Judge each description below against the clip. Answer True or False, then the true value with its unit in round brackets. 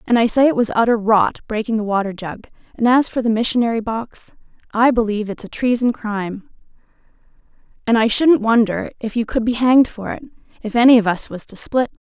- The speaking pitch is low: False (225 Hz)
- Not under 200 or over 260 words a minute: True (205 wpm)